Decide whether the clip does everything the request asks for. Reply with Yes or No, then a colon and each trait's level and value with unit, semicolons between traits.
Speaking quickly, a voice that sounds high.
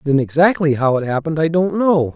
No: fast, 220 wpm; medium, 155 Hz